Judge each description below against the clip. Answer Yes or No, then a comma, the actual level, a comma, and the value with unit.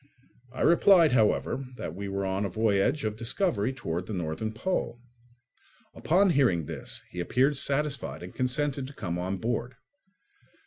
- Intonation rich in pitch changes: Yes, wide, 6.2 semitones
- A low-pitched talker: Yes, low, 115 Hz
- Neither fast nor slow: Yes, average, 150 wpm